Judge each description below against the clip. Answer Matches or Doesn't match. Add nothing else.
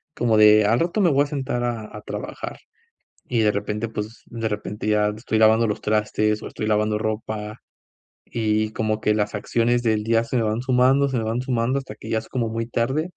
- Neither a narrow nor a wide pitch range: Doesn't match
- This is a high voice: Doesn't match